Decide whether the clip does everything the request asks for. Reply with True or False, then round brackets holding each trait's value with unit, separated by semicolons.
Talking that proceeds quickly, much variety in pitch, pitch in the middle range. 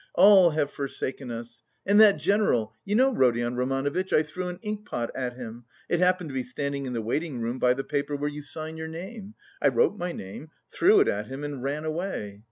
True (215 wpm; 6.4 semitones; 145 Hz)